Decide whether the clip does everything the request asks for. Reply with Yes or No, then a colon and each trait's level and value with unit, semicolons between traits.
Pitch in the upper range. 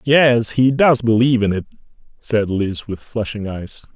No: low, 115 Hz